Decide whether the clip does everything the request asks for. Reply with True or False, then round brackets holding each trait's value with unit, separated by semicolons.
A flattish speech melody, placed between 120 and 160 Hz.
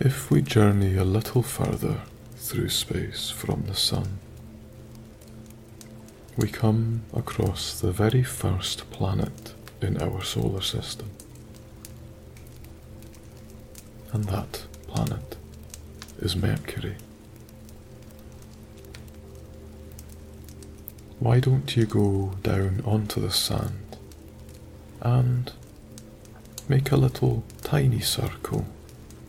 False (2.2 semitones; 110 Hz)